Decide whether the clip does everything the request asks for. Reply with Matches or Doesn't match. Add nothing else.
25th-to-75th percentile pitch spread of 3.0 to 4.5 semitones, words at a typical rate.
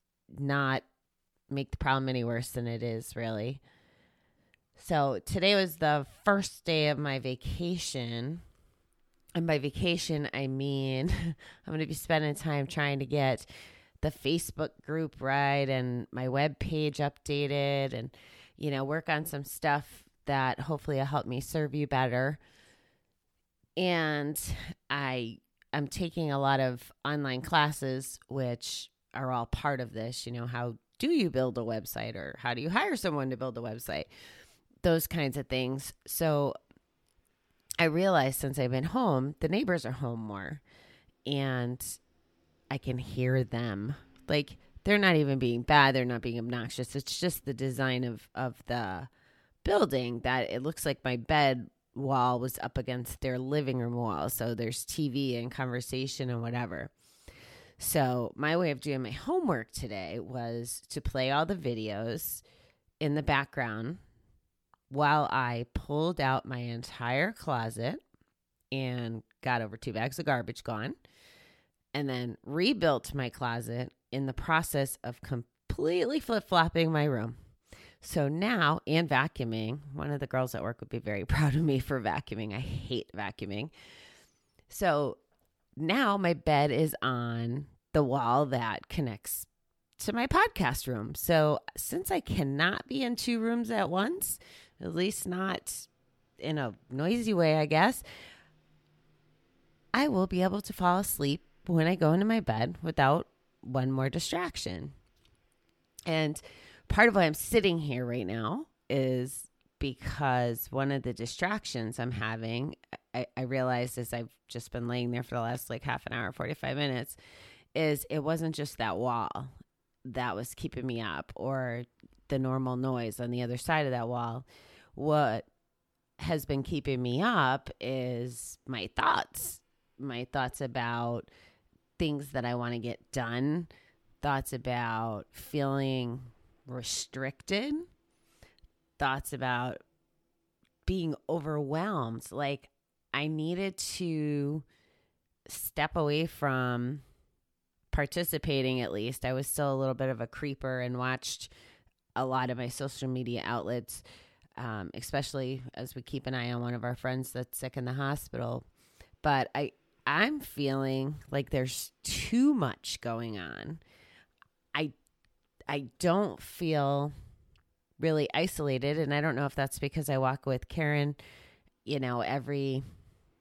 Matches